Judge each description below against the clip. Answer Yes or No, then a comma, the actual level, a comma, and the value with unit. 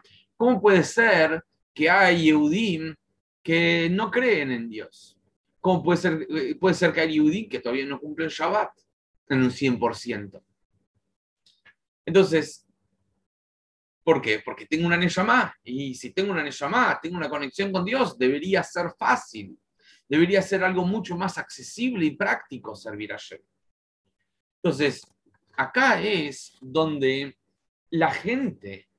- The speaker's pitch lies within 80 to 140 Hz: No, medium, 155 Hz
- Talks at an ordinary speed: No, slow, 130 wpm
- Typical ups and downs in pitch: No, wide, 7.2 semitones